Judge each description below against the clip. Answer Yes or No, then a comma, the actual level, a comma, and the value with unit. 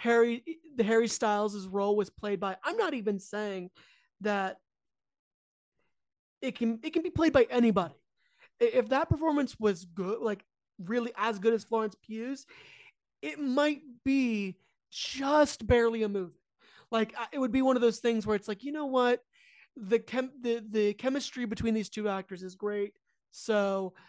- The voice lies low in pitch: No, high, 230 Hz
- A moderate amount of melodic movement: Yes, average, 4.1 semitones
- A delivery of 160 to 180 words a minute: Yes, average, 165 wpm